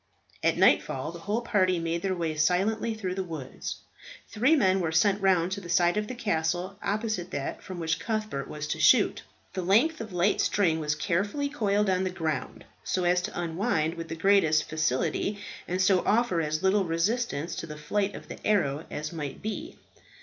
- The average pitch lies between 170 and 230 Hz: Yes, medium, 185 Hz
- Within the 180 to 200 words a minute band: Yes, average, 195 wpm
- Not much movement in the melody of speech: No, average, 4.1 semitones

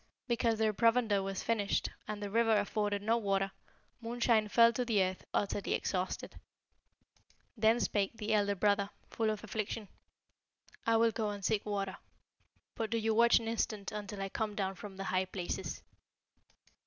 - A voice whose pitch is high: Yes, high, 210 Hz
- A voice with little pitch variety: Yes, narrow, 2.2 semitones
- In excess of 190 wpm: No, average, 165 wpm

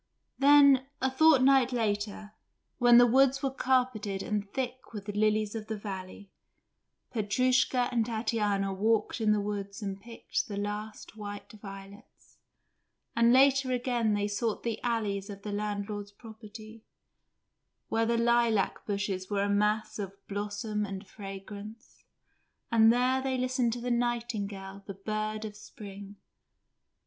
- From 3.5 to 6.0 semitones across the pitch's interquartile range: No, average, 2.9 semitones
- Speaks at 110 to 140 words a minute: Yes, slow, 135 wpm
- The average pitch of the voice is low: No, high, 215 Hz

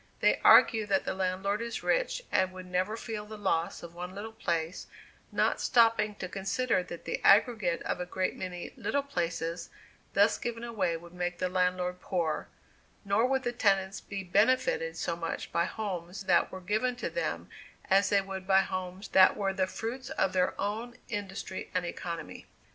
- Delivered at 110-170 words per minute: No, average, 180 wpm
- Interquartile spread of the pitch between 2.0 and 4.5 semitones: Yes, average, 3.5 semitones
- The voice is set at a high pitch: Yes, high, 195 Hz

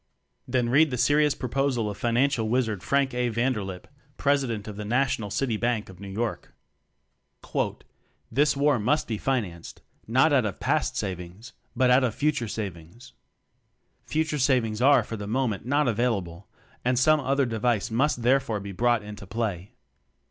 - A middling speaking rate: Yes, average, 165 wpm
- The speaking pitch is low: Yes, low, 120 Hz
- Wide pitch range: No, average, 4.2 semitones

